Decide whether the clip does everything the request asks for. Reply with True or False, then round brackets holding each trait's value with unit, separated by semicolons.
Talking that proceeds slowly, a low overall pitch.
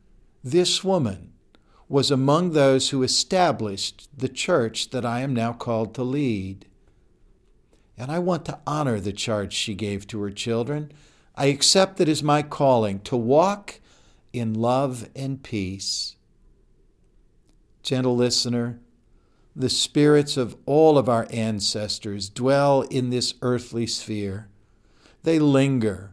True (130 wpm; 125 Hz)